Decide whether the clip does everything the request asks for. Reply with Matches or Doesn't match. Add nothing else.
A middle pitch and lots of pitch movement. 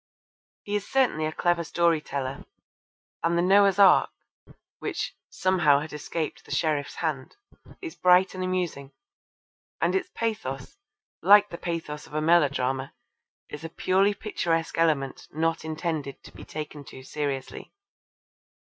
Doesn't match